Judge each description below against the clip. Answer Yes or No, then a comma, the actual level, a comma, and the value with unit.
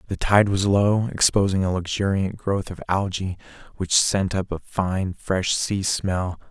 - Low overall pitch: Yes, very low, 95 Hz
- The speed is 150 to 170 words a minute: Yes, average, 165 wpm